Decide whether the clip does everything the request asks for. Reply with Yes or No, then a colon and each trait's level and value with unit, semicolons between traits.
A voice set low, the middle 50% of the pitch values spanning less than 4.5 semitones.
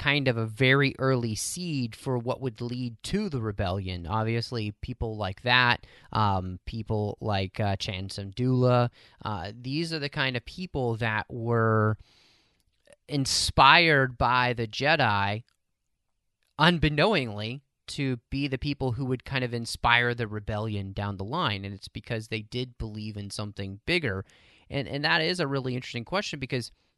Yes: low, 120 Hz; average, 3.9 semitones